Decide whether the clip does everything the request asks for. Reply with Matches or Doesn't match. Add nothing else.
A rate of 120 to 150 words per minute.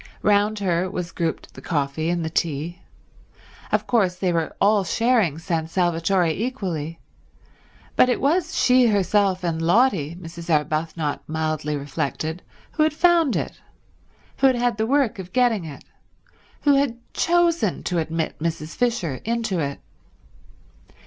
Matches